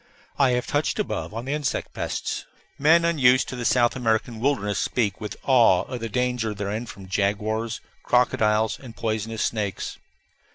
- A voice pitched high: No, low, 115 Hz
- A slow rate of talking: No, average, 160 wpm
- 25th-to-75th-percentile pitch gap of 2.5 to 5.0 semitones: Yes, average, 3.0 semitones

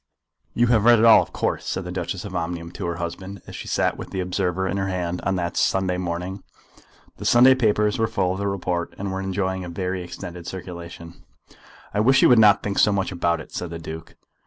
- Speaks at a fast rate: Yes, fast, 230 wpm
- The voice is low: Yes, very low, 95 Hz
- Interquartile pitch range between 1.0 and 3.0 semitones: Yes, narrow, 2.6 semitones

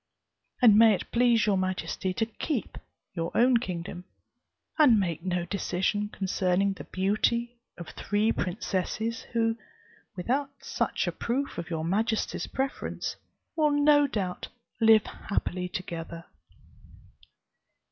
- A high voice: Yes, high, 205 Hz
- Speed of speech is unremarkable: No, slow, 120 wpm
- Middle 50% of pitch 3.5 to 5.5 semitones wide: Yes, average, 4.4 semitones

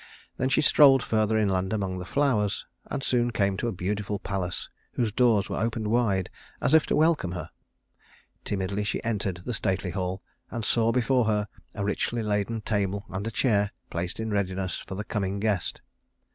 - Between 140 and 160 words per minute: No, average, 180 wpm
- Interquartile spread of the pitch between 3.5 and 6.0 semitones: No, average, 3.1 semitones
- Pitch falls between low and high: No, low, 105 Hz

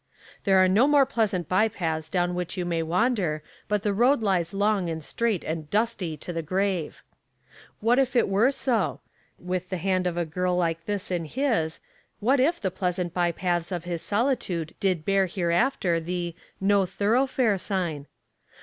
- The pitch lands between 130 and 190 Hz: Yes, medium, 185 Hz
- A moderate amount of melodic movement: Yes, average, 3.7 semitones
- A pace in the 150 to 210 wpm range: Yes, average, 175 wpm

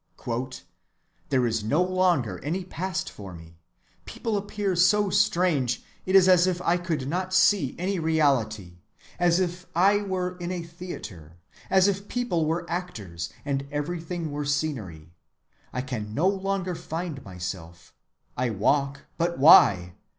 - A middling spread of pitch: No, wide, 6.9 semitones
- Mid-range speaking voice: Yes, medium, 165 Hz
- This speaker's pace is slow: No, average, 145 wpm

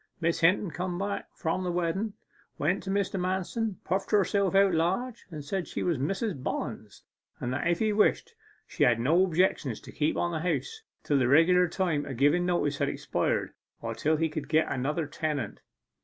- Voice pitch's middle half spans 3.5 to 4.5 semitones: Yes, average, 4.0 semitones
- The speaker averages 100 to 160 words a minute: No, average, 190 wpm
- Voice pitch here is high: No, medium, 175 Hz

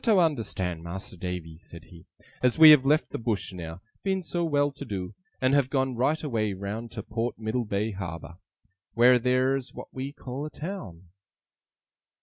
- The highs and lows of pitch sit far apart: Yes, wide, 6.9 semitones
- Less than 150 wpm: No, average, 180 wpm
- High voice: No, low, 120 Hz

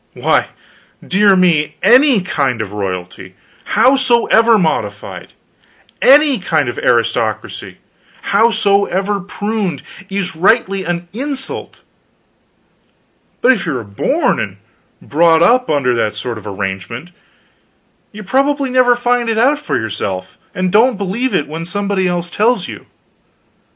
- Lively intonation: Yes, wide, 7.9 semitones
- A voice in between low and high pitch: No, high, 195 Hz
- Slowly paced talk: Yes, slow, 125 wpm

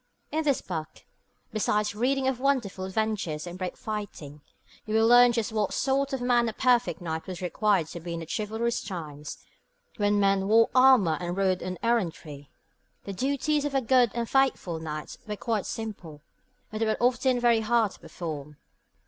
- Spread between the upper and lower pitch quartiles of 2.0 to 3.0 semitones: No, wide, 5.6 semitones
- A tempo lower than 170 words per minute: No, average, 180 wpm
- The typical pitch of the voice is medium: No, high, 215 Hz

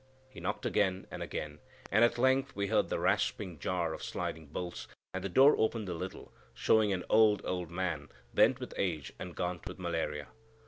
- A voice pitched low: Yes, very low, 95 Hz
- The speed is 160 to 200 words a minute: Yes, average, 190 wpm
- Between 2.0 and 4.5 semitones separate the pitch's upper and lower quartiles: Yes, average, 3.9 semitones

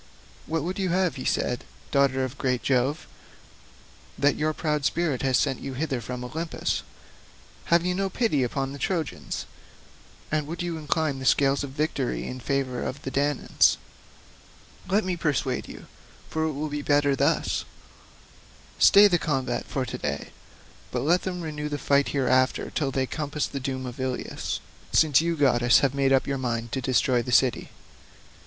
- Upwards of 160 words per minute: Yes, average, 170 wpm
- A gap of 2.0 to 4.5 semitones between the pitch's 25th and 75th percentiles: Yes, average, 3.3 semitones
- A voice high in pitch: No, medium, 140 Hz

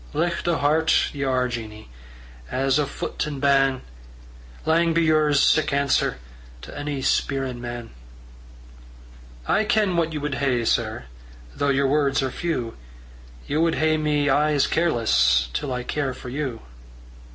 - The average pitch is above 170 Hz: No, medium, 140 Hz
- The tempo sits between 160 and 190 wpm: No, average, 150 wpm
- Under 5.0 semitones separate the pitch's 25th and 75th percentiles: Yes, average, 3.2 semitones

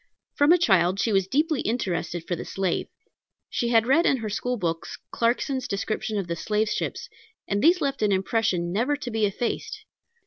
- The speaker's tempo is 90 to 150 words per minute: No, average, 185 wpm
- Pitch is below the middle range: No, high, 220 Hz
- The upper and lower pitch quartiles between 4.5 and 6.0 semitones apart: Yes, average, 5.0 semitones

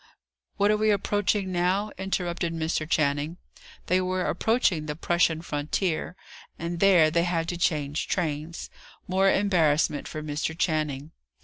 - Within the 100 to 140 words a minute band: Yes, slow, 135 wpm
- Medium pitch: Yes, medium, 170 Hz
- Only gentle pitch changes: No, average, 3.3 semitones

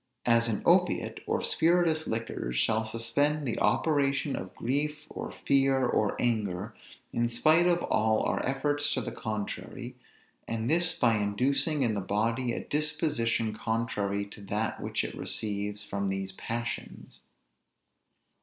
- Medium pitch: No, low, 115 Hz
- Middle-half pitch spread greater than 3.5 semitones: Yes, average, 5.1 semitones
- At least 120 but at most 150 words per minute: Yes, average, 140 wpm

